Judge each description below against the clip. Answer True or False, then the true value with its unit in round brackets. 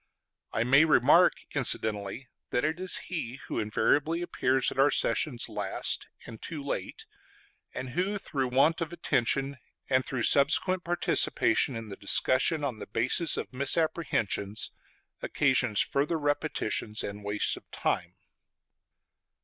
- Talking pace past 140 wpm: False (135 wpm)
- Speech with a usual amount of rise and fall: False (5.7 semitones)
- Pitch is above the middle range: False (135 Hz)